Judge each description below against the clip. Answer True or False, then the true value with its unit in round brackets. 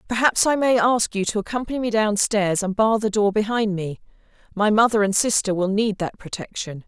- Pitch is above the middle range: True (210 Hz)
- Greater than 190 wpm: True (200 wpm)